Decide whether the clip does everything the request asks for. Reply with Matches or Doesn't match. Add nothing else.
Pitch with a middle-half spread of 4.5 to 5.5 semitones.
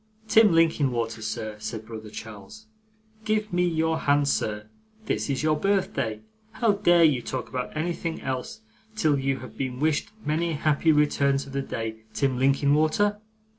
Matches